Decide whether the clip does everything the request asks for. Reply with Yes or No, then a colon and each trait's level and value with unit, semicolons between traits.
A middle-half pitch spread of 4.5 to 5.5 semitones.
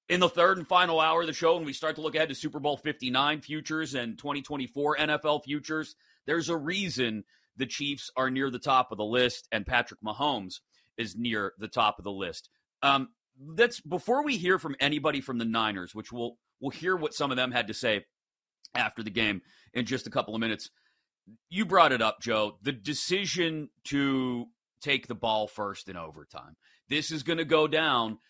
Yes: average, 5.1 semitones